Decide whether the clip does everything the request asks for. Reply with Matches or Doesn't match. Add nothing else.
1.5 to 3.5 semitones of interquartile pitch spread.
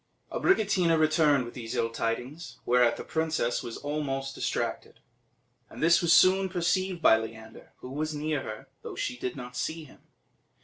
Doesn't match